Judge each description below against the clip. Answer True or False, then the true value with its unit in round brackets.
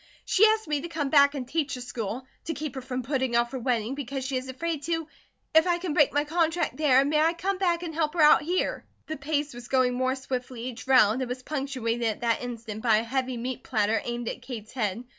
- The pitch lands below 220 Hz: False (265 Hz)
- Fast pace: True (245 wpm)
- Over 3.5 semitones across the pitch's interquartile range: True (3.9 semitones)